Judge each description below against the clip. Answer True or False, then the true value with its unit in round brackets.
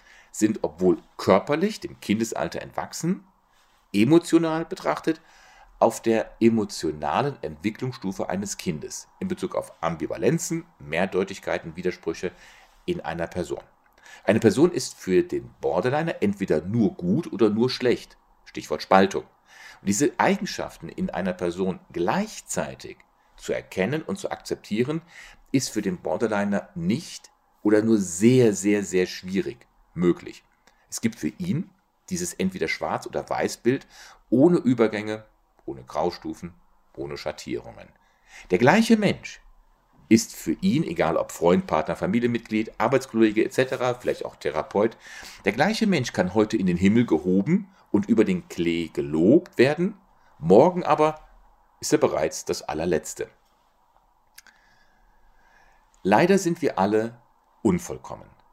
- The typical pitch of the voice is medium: False (130 Hz)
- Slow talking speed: True (120 wpm)